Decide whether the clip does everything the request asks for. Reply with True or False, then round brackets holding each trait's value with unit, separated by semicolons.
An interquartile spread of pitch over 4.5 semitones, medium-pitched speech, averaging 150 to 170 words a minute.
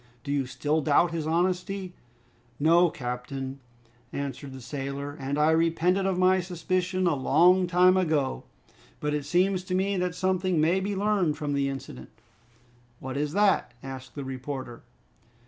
True (4.9 semitones; 160 Hz; 155 wpm)